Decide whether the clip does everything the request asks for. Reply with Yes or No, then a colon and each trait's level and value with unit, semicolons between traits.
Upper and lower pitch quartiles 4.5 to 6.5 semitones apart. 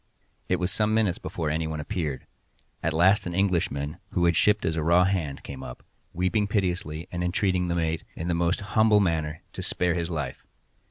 No: average, 2.9 semitones